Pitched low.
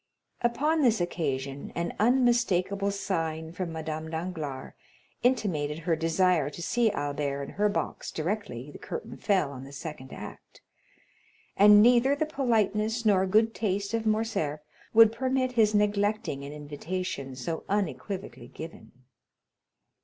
No: medium, 185 Hz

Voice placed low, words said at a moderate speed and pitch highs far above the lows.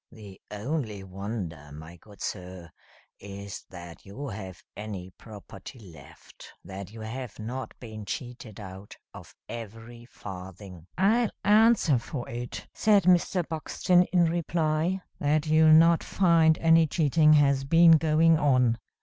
No: low, 120 Hz; slow, 130 wpm; wide, 8.4 semitones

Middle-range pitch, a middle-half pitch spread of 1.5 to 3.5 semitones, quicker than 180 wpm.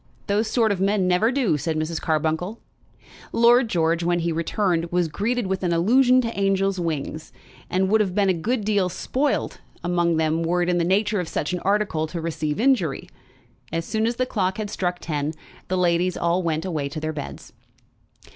No: medium, 180 Hz; average, 4.0 semitones; average, 195 wpm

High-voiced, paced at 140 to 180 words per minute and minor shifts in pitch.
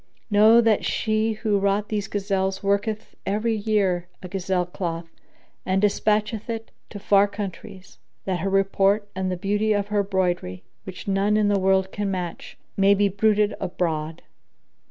Yes: high, 200 Hz; average, 155 wpm; narrow, 1.8 semitones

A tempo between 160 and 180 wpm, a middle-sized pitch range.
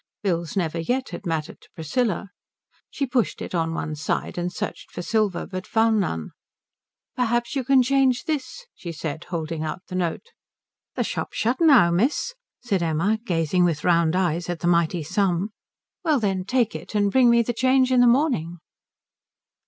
No: average, 175 wpm; wide, 6.5 semitones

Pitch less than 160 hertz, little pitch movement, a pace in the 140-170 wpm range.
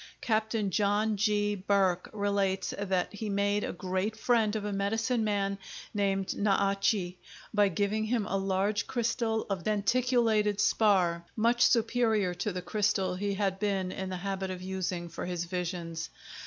No: high, 200 Hz; narrow, 2.3 semitones; average, 160 wpm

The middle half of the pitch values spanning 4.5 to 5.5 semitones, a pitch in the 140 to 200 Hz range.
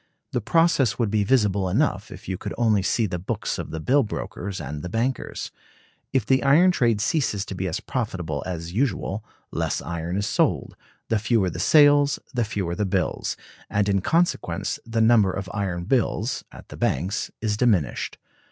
No: average, 4.8 semitones; low, 105 Hz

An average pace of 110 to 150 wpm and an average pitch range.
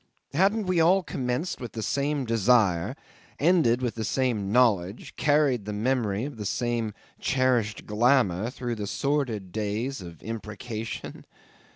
Yes: average, 140 wpm; average, 4.2 semitones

